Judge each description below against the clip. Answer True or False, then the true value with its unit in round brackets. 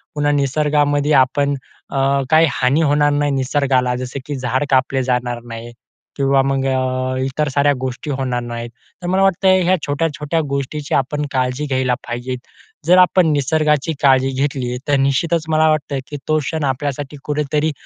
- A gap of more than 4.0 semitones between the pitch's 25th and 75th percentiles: False (2.5 semitones)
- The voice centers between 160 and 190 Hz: False (140 Hz)